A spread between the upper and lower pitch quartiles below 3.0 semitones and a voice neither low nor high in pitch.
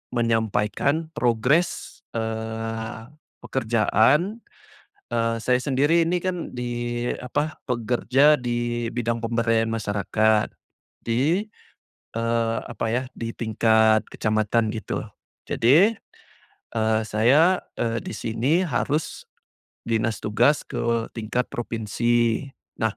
No: narrow, 2.4 semitones; low, 115 Hz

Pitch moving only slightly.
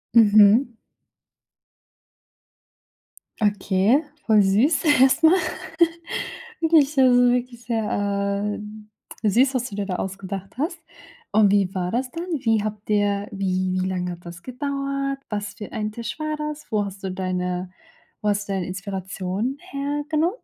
No: wide, 5.4 semitones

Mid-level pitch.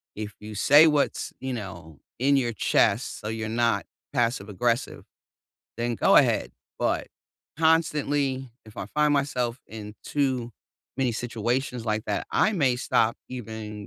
No: low, 120 Hz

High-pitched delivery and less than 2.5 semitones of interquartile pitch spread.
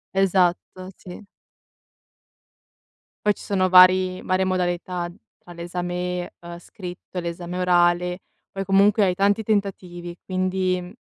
No: medium, 180 Hz; narrow, 1.2 semitones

